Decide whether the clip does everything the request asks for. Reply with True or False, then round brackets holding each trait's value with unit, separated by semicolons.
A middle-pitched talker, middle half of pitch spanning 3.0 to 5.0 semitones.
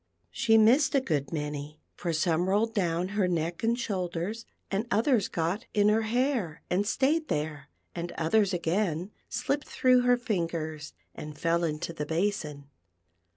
False (180 Hz; 5.5 semitones)